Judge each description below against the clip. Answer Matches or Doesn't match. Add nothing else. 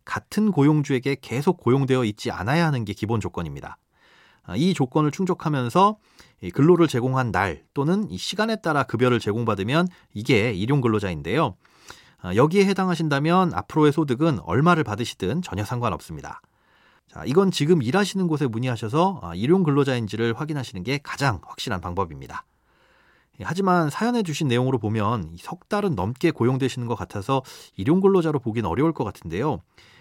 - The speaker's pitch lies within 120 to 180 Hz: Matches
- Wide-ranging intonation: Matches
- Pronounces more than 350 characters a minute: Matches